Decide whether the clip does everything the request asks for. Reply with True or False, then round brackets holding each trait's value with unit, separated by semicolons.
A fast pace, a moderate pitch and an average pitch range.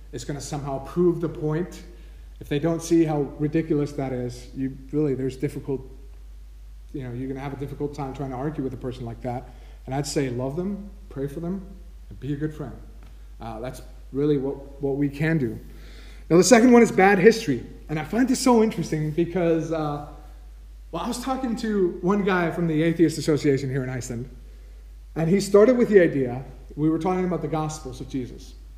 True (210 wpm; 145 Hz; 4.6 semitones)